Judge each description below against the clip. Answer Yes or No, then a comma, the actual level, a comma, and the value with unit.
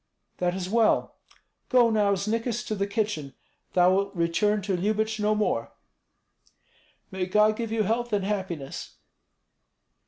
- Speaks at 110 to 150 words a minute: Yes, slow, 135 wpm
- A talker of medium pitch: No, high, 210 Hz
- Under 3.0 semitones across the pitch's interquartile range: Yes, narrow, 2.6 semitones